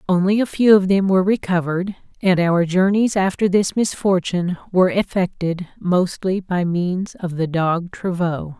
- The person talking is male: No, female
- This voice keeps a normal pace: Yes, average, 155 wpm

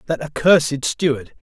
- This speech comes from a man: Yes, male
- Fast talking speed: No, slow, 120 wpm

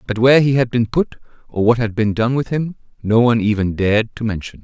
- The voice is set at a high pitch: No, low, 115 Hz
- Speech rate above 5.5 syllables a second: Yes, 6.1 syllables/s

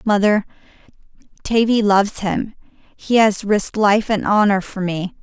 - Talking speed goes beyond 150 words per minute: No, average, 140 wpm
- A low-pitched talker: No, high, 205 Hz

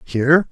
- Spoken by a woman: No, male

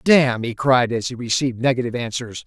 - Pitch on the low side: Yes, low, 125 Hz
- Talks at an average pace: Yes, average, 195 wpm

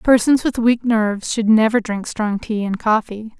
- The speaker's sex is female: Yes, female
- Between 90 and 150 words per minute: No, average, 195 wpm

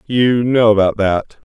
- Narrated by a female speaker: No, male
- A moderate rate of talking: Yes, average, 160 wpm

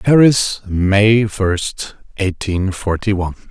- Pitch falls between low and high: No, low, 100 Hz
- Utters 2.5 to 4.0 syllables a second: Yes, 3.2 syllables/s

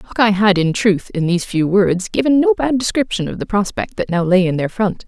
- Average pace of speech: No, fast, 250 wpm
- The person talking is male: No, female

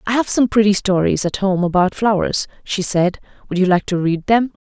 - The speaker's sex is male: No, female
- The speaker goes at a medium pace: No, fast, 220 wpm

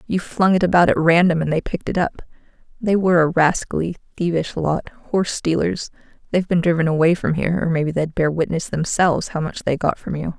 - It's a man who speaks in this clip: No, female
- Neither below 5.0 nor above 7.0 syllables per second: Yes, 6.0 syllables/s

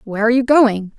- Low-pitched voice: No, high, 230 Hz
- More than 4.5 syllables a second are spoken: Yes, 7.0 syllables/s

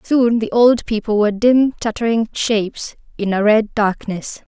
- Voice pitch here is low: No, high, 225 Hz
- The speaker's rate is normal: Yes, average, 160 wpm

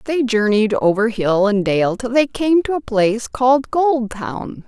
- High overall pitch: Yes, high, 235 Hz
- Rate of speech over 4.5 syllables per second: No, 4.3 syllables/s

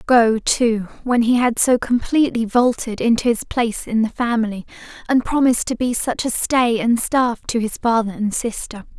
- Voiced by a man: No, female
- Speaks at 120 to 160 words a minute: No, average, 185 wpm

